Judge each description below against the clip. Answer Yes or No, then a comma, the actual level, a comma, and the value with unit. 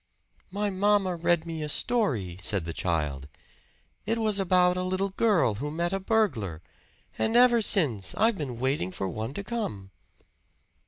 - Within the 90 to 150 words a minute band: No, average, 160 wpm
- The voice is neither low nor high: Yes, medium, 175 Hz